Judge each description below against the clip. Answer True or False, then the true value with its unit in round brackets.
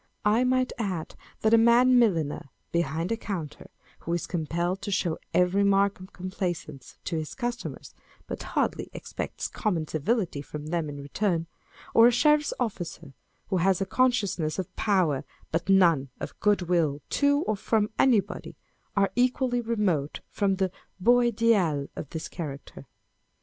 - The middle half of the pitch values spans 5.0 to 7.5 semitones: True (5.6 semitones)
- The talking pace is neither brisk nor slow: True (155 wpm)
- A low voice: False (190 Hz)